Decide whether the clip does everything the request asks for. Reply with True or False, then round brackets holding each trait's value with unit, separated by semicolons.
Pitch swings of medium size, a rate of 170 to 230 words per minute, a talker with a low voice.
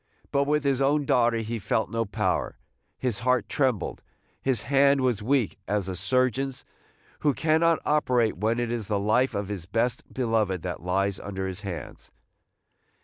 True (4.7 semitones; 175 wpm; 115 Hz)